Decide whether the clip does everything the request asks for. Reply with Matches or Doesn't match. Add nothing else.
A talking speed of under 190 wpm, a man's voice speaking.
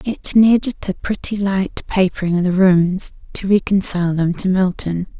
Doesn't match